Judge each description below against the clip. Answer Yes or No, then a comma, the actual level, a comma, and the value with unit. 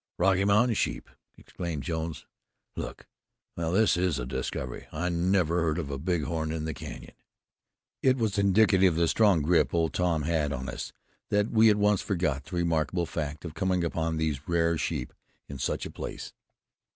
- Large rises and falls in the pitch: No, average, 3.3 semitones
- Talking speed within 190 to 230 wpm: No, average, 175 wpm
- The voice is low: Yes, very low, 85 Hz